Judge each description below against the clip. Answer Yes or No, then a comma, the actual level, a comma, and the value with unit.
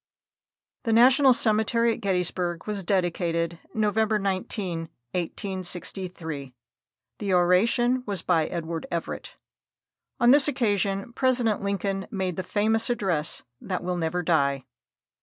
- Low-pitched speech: No, high, 190 Hz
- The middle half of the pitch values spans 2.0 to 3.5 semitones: No, average, 4.2 semitones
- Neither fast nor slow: No, slow, 115 wpm